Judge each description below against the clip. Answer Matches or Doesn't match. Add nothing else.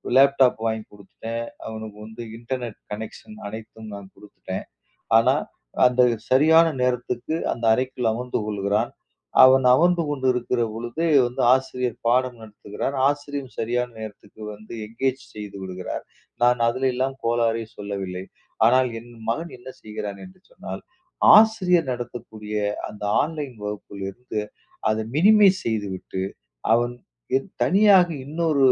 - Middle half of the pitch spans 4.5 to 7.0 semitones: Doesn't match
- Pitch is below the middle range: Matches